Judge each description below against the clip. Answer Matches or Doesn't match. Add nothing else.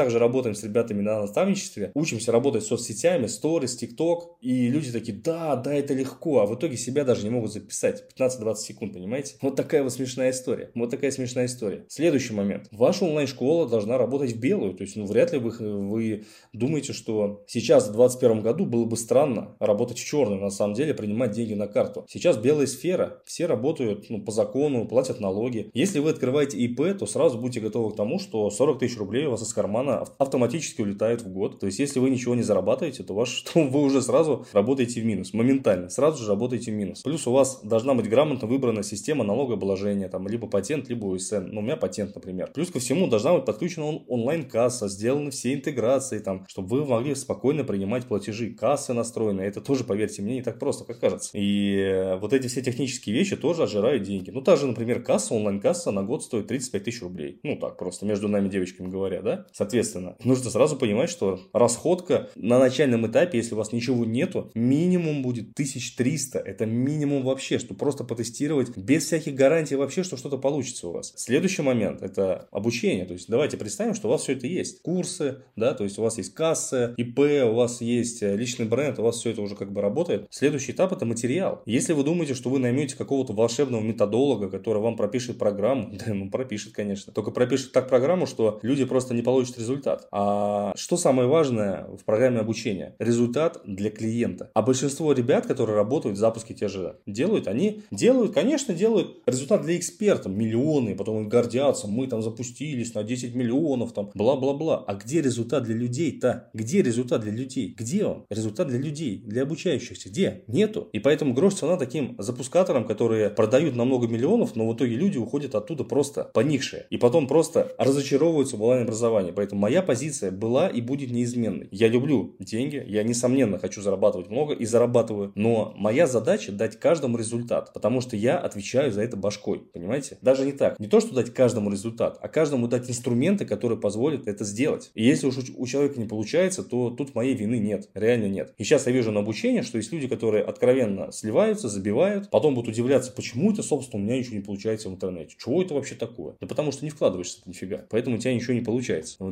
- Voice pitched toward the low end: Matches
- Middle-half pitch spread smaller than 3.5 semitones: Doesn't match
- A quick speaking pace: Matches